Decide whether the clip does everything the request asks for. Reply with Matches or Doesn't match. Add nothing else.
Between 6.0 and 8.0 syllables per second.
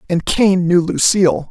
Doesn't match